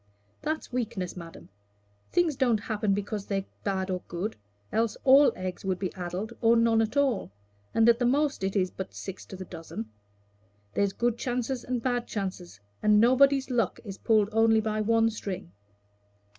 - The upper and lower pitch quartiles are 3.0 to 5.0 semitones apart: Yes, average, 4.0 semitones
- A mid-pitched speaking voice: No, high, 220 Hz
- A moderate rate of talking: Yes, average, 170 wpm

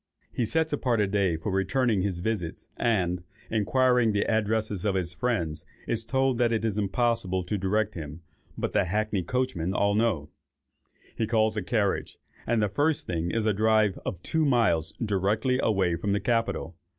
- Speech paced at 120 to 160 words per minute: No, average, 175 wpm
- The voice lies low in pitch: Yes, low, 105 Hz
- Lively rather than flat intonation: No, average, 3.7 semitones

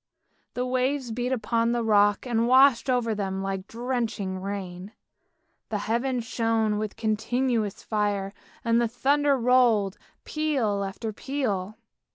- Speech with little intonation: No, average, 3.4 semitones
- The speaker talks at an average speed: No, slow, 130 wpm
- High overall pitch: Yes, high, 230 Hz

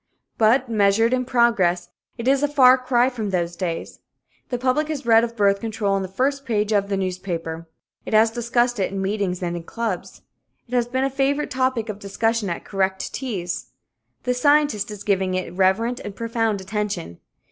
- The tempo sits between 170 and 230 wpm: Yes, average, 190 wpm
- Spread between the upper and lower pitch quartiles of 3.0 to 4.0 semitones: No, average, 4.5 semitones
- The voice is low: No, high, 220 Hz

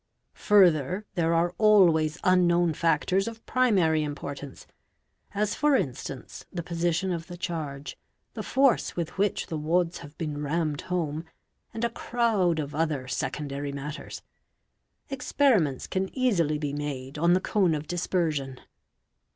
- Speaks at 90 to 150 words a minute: Yes, average, 140 wpm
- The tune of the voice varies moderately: Yes, average, 4.1 semitones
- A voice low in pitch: No, medium, 165 Hz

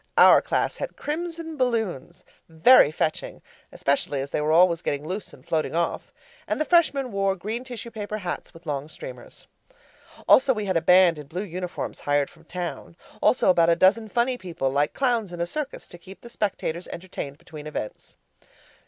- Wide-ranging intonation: Yes, wide, 6.6 semitones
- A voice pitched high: No, medium, 180 Hz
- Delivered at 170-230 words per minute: Yes, average, 180 wpm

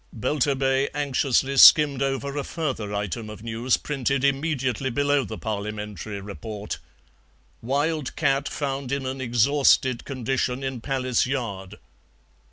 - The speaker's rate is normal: No, slow, 120 wpm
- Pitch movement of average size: Yes, average, 3.6 semitones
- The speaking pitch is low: Yes, low, 130 Hz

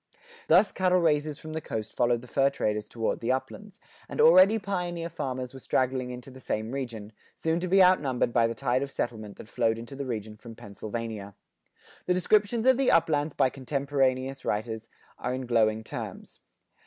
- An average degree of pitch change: No, wide, 5.8 semitones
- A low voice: Yes, low, 130 Hz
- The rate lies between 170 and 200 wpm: Yes, average, 180 wpm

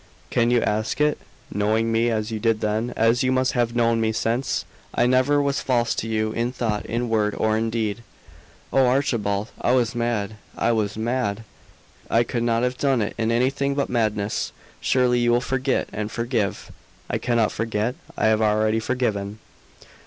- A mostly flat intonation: Yes, narrow, 2.2 semitones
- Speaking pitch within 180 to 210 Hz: No, low, 115 Hz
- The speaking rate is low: No, average, 180 wpm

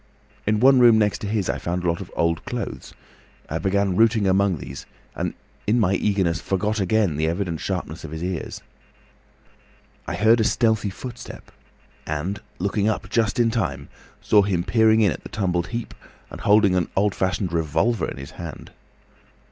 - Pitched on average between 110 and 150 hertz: No, low, 100 Hz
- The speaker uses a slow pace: No, average, 180 wpm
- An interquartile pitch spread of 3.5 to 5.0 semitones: Yes, average, 4.2 semitones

